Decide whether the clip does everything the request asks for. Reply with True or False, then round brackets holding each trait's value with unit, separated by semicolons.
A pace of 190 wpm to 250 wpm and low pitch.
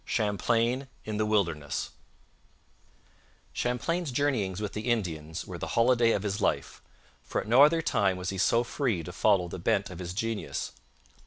False (165 wpm; 105 Hz)